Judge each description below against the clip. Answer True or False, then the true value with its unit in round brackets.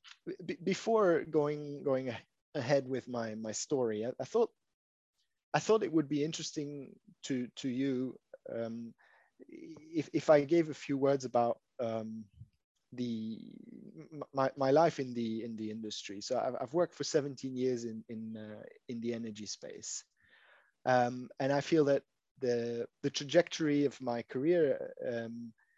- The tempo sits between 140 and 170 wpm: True (150 wpm)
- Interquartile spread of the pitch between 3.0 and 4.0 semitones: False (5.0 semitones)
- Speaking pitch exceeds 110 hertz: True (135 Hz)